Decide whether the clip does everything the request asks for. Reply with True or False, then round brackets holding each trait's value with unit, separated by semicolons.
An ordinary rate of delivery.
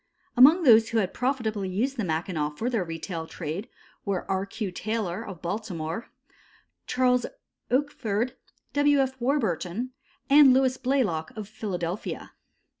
False (130 wpm)